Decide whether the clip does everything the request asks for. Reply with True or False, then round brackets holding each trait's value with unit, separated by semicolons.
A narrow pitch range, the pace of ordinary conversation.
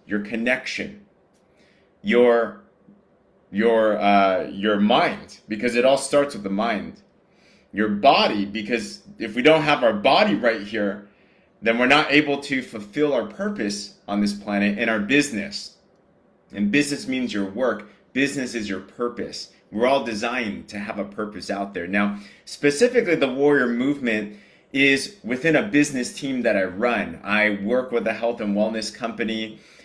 False (5.0 semitones; 155 wpm)